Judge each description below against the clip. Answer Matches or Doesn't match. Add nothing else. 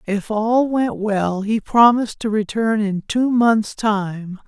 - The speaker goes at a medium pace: Matches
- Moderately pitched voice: Doesn't match